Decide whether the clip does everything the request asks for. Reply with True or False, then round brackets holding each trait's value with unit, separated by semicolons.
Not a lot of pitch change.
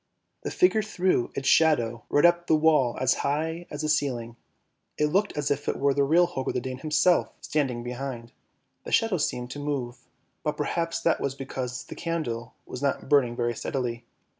False (4.4 semitones)